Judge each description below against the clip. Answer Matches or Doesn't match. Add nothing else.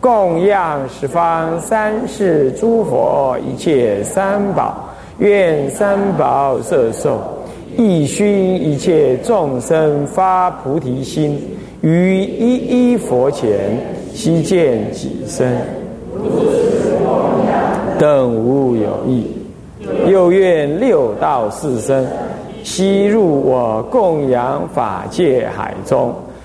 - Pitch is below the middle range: Doesn't match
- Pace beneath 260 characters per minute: Matches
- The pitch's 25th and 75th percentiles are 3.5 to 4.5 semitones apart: Doesn't match